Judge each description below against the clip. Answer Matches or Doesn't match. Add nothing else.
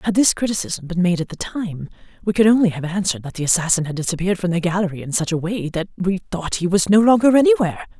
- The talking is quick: Matches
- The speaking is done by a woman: Matches